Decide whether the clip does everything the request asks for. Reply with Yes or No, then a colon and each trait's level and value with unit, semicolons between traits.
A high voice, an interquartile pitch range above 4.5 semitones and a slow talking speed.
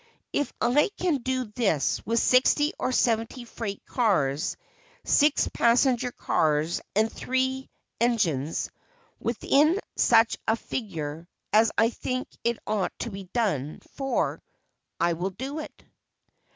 Yes: high, 230 Hz; average, 5.2 semitones; slow, 125 wpm